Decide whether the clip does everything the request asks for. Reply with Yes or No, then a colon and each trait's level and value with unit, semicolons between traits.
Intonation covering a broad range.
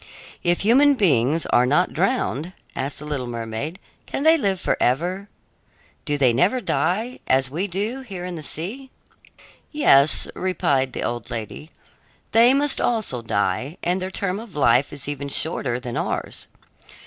Yes: wide, 7.4 semitones